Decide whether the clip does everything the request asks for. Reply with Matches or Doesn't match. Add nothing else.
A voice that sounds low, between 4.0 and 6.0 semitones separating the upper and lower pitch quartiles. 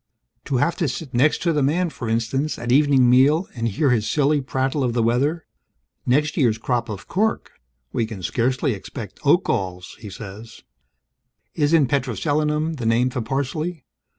Matches